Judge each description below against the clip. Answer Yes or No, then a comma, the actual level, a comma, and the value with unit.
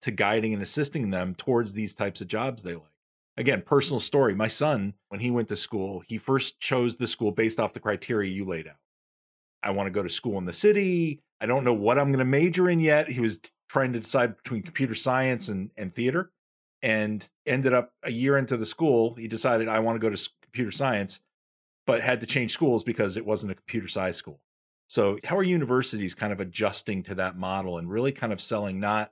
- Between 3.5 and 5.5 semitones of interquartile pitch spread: Yes, average, 4.4 semitones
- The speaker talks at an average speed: No, fast, 225 wpm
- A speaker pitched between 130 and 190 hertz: No, low, 115 Hz